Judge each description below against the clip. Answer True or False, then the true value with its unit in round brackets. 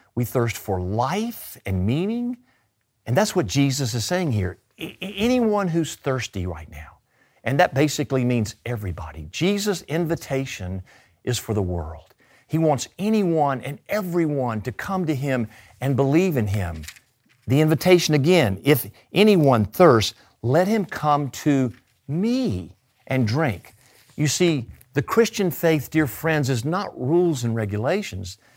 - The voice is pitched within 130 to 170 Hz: True (135 Hz)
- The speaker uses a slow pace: False (145 wpm)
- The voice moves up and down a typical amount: False (7.3 semitones)